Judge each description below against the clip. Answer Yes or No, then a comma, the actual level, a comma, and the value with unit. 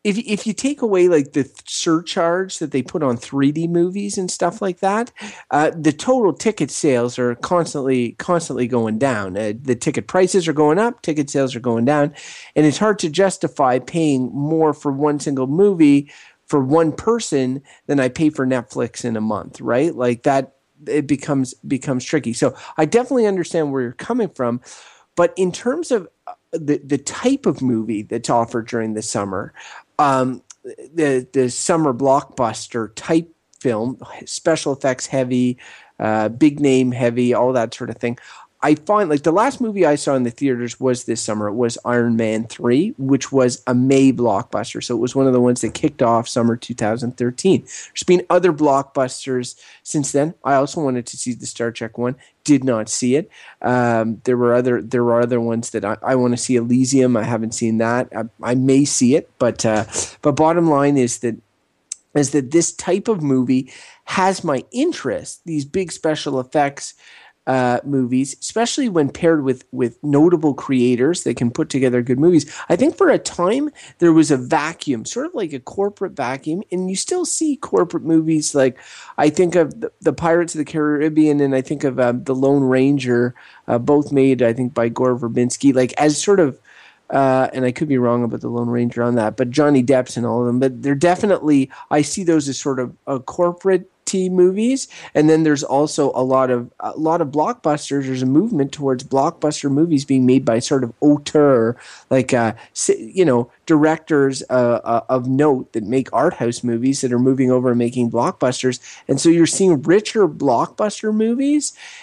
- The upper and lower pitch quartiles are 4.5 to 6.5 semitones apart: Yes, average, 4.8 semitones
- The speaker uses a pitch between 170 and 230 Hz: No, low, 135 Hz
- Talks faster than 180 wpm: Yes, average, 195 wpm